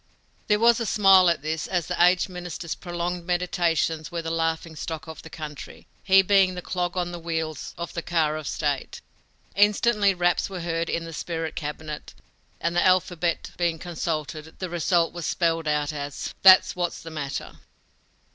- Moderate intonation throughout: No, narrow, 2.0 semitones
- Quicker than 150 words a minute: Yes, average, 175 wpm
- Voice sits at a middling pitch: Yes, medium, 170 Hz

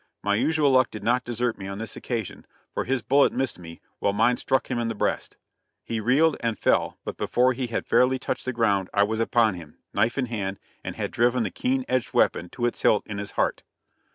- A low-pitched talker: Yes, low, 115 Hz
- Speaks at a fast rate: Yes, fast, 230 wpm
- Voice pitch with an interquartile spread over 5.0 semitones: No, average, 3.6 semitones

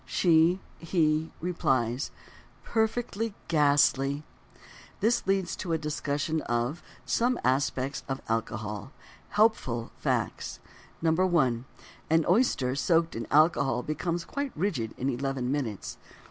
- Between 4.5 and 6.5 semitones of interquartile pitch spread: Yes, average, 5.1 semitones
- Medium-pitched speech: Yes, medium, 150 Hz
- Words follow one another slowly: Yes, slow, 105 wpm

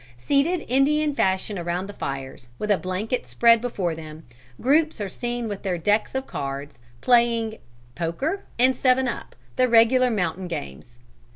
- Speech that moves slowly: No, average, 165 wpm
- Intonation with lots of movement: Yes, wide, 6.6 semitones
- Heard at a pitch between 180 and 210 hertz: No, high, 220 Hz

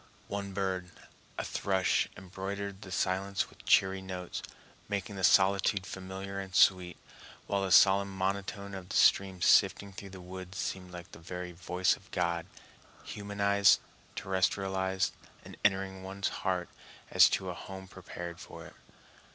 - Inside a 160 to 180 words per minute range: No, average, 145 wpm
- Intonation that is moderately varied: No, narrow, 1.1 semitones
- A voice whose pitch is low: Yes, very low, 95 Hz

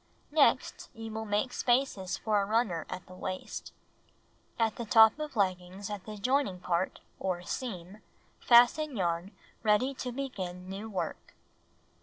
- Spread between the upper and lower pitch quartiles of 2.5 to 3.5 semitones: No, average, 4.6 semitones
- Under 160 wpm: Yes, average, 145 wpm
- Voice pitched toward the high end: Yes, high, 210 Hz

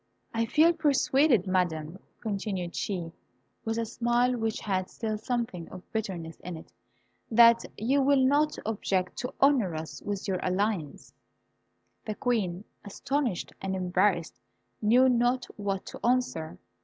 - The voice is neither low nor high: No, high, 215 Hz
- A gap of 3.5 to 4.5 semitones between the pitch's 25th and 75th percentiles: No, average, 5.0 semitones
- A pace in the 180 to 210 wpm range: No, slow, 135 wpm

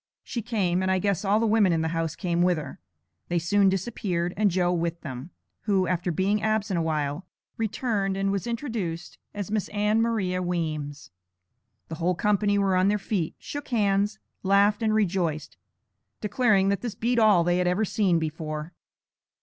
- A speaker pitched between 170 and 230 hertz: Yes, high, 190 Hz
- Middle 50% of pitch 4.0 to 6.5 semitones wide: No, average, 3.6 semitones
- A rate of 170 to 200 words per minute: Yes, average, 180 wpm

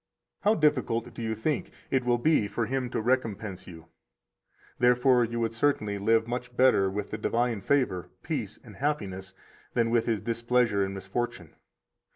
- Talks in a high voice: No, low, 115 Hz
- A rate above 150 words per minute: Yes, average, 165 wpm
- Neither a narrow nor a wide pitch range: Yes, average, 3.4 semitones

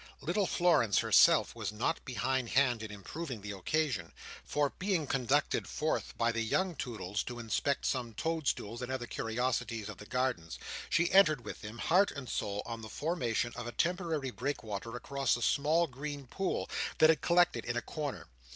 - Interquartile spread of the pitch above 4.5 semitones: Yes, average, 5.3 semitones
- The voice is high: No, low, 130 Hz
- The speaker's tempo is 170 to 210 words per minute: Yes, average, 180 wpm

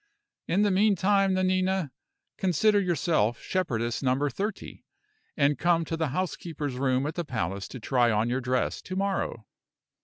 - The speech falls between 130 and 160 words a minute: Yes, average, 150 wpm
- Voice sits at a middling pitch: Yes, medium, 165 Hz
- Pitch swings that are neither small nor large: No, wide, 6.6 semitones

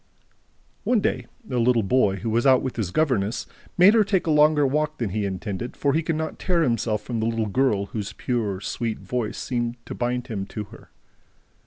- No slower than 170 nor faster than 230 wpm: Yes, fast, 205 wpm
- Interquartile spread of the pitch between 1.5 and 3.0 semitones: No, wide, 5.5 semitones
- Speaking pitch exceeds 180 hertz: No, low, 120 Hz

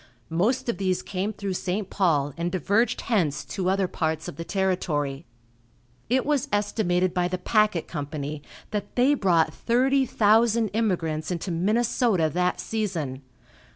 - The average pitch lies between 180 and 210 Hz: Yes, medium, 185 Hz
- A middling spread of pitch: Yes, average, 4.7 semitones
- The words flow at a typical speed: Yes, average, 145 wpm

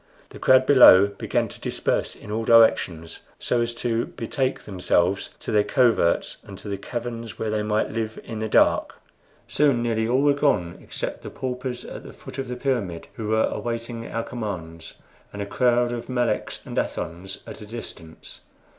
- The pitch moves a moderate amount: Yes, average, 3.2 semitones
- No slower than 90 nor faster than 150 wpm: No, average, 180 wpm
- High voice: No, low, 115 Hz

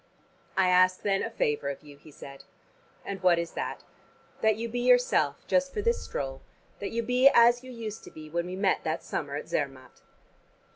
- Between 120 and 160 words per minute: No, average, 200 wpm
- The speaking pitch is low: No, high, 195 Hz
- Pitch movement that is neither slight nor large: No, wide, 6.8 semitones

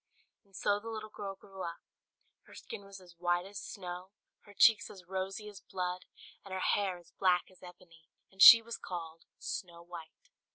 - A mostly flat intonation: Yes, narrow, 2.2 semitones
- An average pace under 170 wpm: No, average, 190 wpm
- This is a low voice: No, medium, 185 Hz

